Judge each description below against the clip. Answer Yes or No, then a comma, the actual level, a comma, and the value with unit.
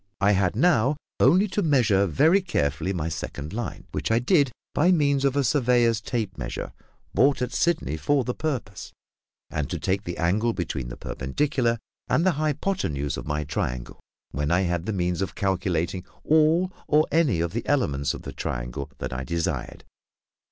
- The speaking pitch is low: Yes, low, 105 Hz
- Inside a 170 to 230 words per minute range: Yes, average, 175 wpm